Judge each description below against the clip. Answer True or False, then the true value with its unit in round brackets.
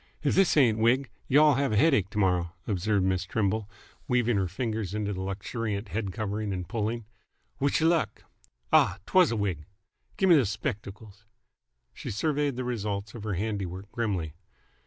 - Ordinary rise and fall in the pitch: True (4.0 semitones)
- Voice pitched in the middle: False (105 Hz)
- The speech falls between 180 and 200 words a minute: False (165 wpm)